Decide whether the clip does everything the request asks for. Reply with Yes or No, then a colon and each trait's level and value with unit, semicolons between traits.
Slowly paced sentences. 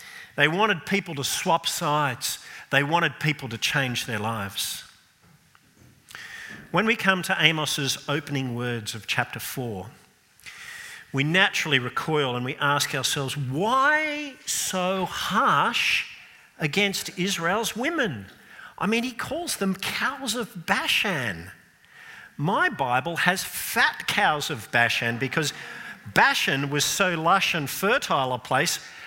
Yes: slow, 125 wpm